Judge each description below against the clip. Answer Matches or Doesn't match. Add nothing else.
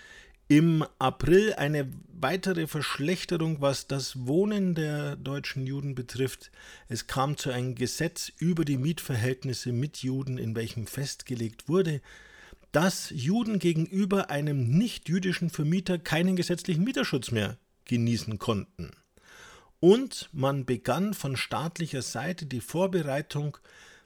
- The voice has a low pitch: Doesn't match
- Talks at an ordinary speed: Doesn't match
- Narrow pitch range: Doesn't match